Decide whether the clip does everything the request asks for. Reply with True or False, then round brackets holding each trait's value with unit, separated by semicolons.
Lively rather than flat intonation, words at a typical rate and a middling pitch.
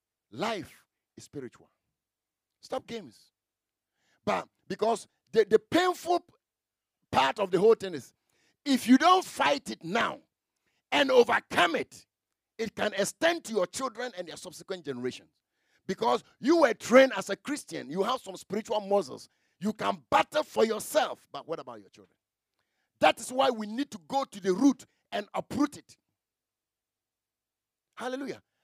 False (6.3 semitones; 150 wpm; 250 Hz)